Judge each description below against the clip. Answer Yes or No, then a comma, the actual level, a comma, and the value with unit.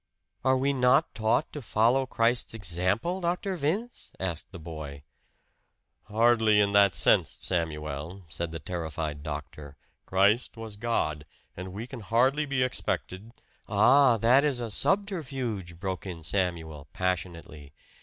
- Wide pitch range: Yes, wide, 7.2 semitones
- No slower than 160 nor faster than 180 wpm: No, slow, 135 wpm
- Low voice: Yes, low, 100 Hz